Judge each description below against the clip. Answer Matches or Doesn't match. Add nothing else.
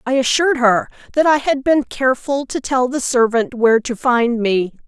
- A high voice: Matches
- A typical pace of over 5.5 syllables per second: Doesn't match